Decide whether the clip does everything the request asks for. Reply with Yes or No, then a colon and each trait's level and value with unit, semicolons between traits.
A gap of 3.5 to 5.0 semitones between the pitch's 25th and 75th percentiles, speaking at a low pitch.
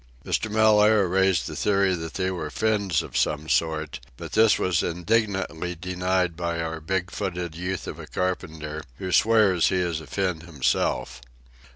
No: average, 2.9 semitones; very low, 90 Hz